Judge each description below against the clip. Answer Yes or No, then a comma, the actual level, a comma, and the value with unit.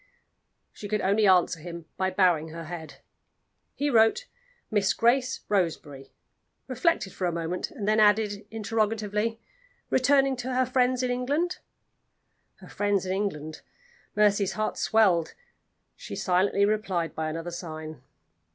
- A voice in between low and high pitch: No, high, 205 Hz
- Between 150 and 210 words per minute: No, slow, 135 wpm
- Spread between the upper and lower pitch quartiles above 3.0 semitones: Yes, average, 4.4 semitones